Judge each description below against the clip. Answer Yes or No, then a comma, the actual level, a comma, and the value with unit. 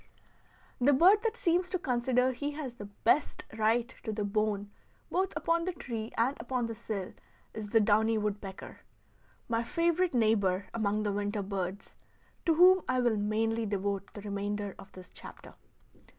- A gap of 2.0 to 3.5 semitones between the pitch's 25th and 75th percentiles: No, average, 4.4 semitones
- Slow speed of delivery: No, average, 165 wpm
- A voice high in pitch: Yes, high, 225 Hz